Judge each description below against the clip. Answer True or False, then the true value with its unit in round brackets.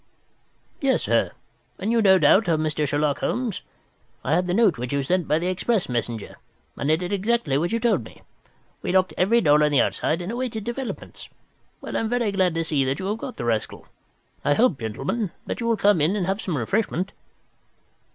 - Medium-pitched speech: True (180 Hz)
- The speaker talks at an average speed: False (210 wpm)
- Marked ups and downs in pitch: True (6.8 semitones)